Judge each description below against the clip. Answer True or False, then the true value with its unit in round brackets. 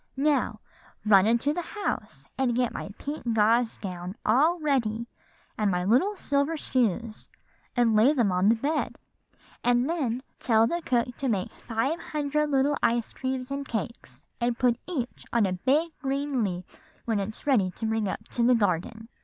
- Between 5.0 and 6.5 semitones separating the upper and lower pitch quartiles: False (4.4 semitones)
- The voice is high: True (240 Hz)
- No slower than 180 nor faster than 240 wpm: False (170 wpm)